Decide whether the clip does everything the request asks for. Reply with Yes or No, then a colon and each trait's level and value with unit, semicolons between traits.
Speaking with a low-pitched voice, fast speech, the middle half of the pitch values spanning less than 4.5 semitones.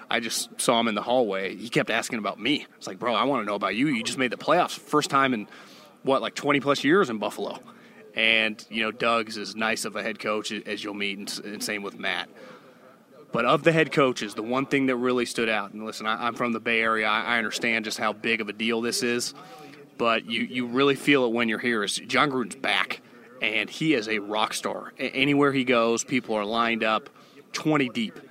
Yes: low, 115 Hz; fast, 240 wpm; average, 2.8 semitones